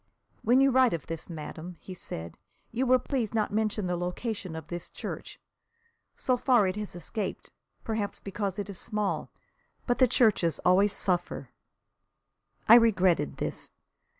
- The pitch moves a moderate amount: Yes, average, 4.5 semitones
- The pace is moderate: Yes, average, 150 wpm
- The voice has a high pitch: Yes, high, 205 Hz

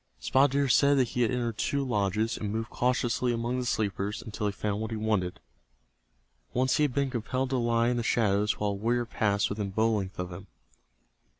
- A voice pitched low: Yes, low, 115 Hz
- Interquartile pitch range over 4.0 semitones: No, average, 3.3 semitones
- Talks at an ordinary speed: No, fast, 210 wpm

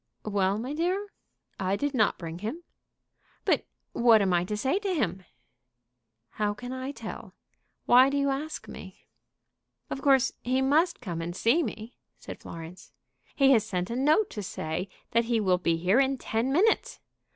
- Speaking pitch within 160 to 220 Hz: No, high, 235 Hz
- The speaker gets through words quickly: No, average, 175 wpm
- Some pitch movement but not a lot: No, wide, 6.2 semitones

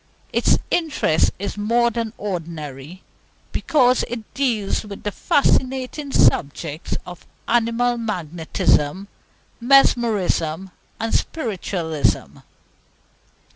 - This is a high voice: Yes, high, 210 Hz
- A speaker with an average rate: No, slow, 85 wpm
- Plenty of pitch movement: Yes, wide, 6.1 semitones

